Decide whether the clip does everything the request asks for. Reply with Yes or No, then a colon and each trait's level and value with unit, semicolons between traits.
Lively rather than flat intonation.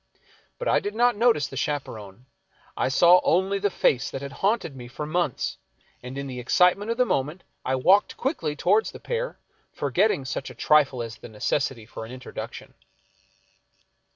Yes: wide, 7.5 semitones